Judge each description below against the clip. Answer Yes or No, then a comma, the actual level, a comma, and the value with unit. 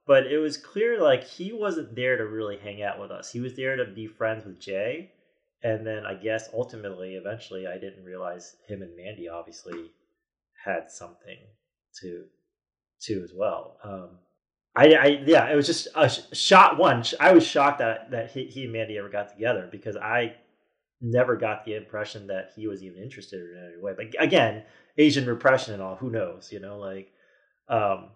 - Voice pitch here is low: Yes, low, 110 Hz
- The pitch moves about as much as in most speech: Yes, average, 4.8 semitones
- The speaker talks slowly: No, average, 190 wpm